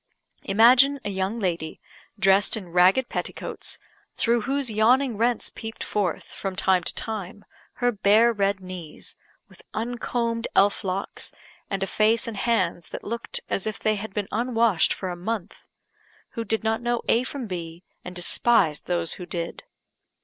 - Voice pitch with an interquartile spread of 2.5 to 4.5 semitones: Yes, average, 3.8 semitones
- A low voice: No, high, 210 Hz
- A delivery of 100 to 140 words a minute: No, average, 160 wpm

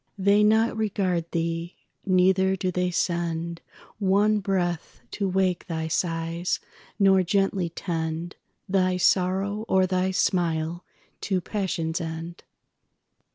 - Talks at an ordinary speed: No, slow, 105 wpm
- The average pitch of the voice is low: No, medium, 185 Hz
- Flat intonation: Yes, narrow, 2.3 semitones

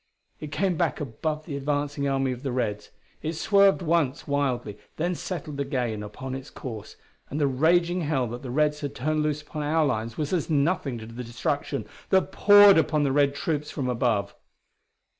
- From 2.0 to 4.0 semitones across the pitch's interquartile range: Yes, average, 3.6 semitones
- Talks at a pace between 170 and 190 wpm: Yes, average, 185 wpm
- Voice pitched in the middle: Yes, medium, 145 Hz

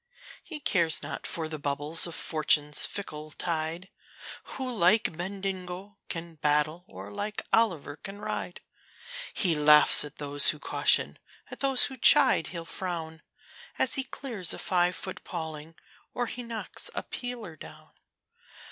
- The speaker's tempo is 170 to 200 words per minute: No, average, 145 wpm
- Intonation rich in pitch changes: No, average, 4.8 semitones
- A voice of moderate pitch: Yes, medium, 170 Hz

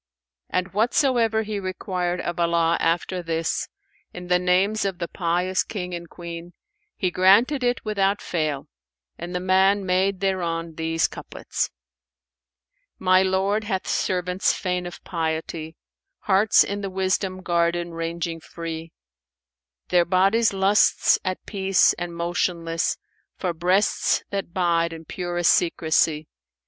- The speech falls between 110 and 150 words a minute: Yes, slow, 135 wpm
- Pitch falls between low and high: Yes, medium, 180 Hz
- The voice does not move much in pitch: Yes, narrow, 2.3 semitones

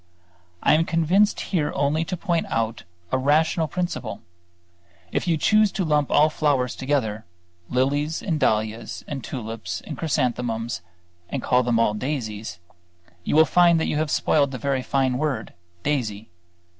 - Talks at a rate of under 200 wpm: Yes, average, 155 wpm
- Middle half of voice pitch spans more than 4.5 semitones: Yes, wide, 5.4 semitones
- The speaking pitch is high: No, medium, 140 Hz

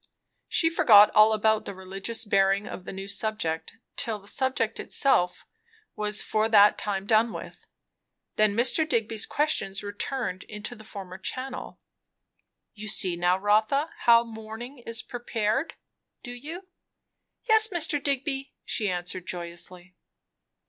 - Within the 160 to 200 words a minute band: No, slow, 135 wpm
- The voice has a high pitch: Yes, high, 215 Hz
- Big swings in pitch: No, average, 4.3 semitones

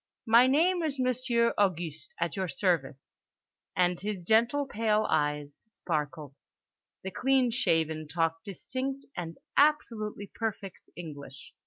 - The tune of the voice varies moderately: No, wide, 7.2 semitones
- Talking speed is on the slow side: Yes, slow, 120 wpm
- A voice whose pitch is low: No, high, 200 Hz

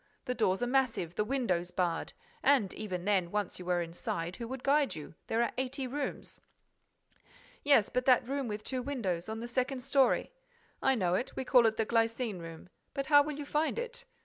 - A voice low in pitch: No, high, 235 Hz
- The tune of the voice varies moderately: No, wide, 6.3 semitones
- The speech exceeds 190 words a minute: Yes, average, 200 wpm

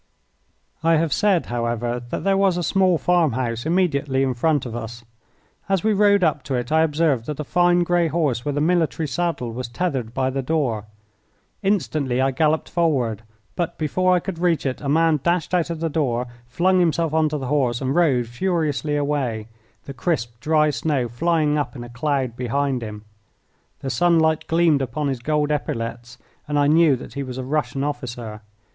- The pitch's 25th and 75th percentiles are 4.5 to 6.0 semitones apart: Yes, average, 4.9 semitones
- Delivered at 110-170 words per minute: No, average, 190 wpm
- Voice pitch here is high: No, medium, 145 Hz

